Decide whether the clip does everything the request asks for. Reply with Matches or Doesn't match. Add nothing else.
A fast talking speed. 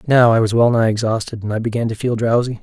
Matches